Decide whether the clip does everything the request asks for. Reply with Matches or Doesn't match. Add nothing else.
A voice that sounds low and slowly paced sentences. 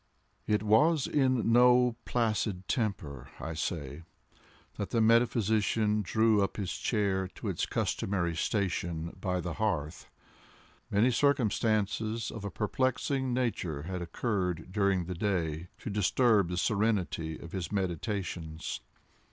Matches